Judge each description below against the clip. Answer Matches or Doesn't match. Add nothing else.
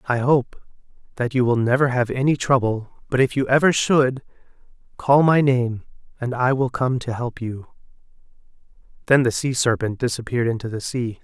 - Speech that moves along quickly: Doesn't match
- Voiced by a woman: Doesn't match